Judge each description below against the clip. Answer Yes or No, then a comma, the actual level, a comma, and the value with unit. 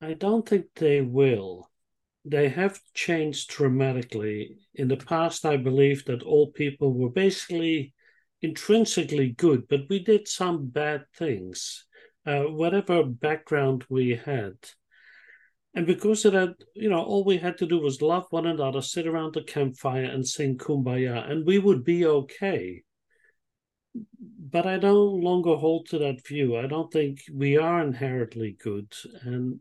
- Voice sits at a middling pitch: Yes, medium, 150 Hz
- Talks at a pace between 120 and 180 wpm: Yes, average, 150 wpm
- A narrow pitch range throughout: No, average, 4.7 semitones